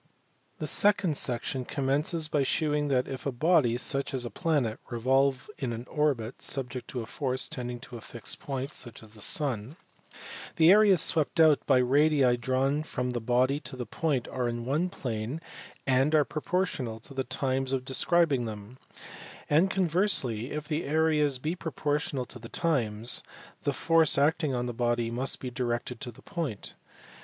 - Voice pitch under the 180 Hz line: Yes, low, 135 Hz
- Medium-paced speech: Yes, average, 160 wpm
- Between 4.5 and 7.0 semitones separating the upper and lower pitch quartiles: No, average, 3.8 semitones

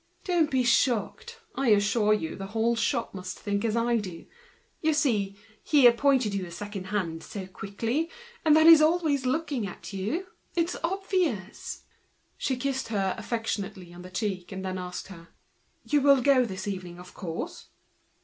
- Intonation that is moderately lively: No, wide, 6.5 semitones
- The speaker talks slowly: No, average, 150 wpm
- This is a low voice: No, high, 220 Hz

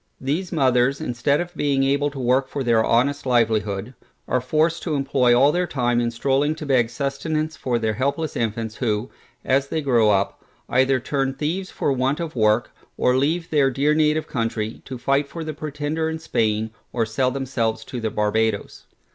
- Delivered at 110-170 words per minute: No, average, 185 wpm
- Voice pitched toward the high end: No, low, 135 Hz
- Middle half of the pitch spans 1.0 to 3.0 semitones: No, average, 3.9 semitones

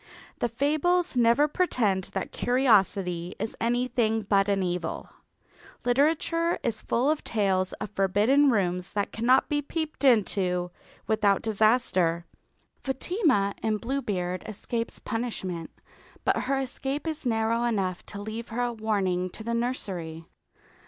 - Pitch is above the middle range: Yes, high, 225 Hz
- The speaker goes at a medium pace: No, slow, 130 wpm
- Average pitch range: Yes, average, 4.9 semitones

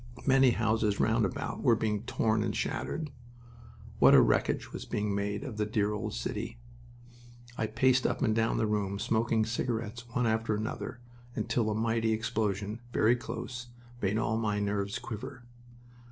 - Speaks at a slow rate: No, average, 160 wpm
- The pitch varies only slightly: Yes, narrow, 1.9 semitones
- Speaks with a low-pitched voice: Yes, low, 110 Hz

